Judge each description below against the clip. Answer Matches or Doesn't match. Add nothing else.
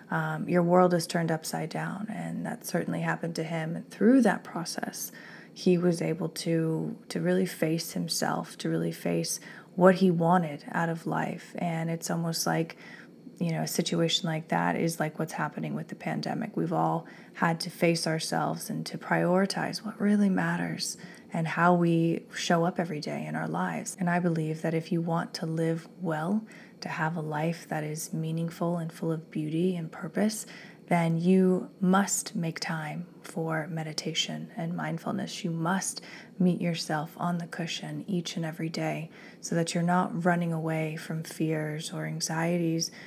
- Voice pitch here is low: Doesn't match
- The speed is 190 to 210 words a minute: Doesn't match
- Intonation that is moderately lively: Doesn't match